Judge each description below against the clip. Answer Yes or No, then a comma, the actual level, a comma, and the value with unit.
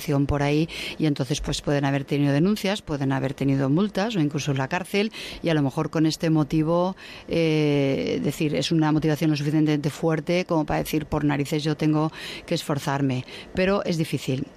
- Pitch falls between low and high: Yes, medium, 155 Hz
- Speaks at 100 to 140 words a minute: No, average, 185 wpm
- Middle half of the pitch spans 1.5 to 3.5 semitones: Yes, narrow, 2.4 semitones